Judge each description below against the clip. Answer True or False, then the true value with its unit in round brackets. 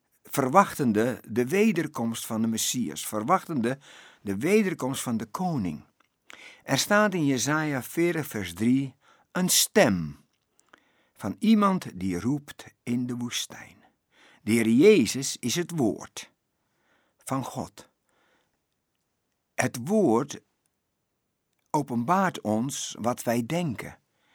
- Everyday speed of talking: False (105 wpm)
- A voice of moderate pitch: False (130 Hz)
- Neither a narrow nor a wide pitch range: False (5.9 semitones)